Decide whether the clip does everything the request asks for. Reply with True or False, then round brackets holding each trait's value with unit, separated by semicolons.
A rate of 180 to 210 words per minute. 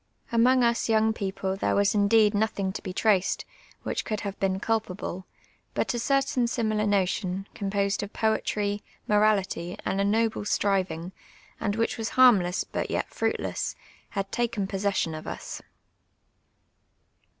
False (140 wpm)